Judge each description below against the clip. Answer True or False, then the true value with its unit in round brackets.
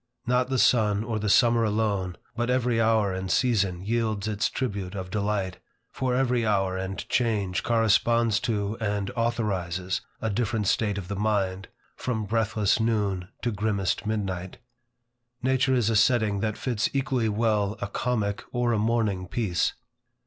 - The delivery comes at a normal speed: True (155 wpm)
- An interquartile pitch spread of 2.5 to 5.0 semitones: True (2.9 semitones)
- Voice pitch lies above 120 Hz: False (110 Hz)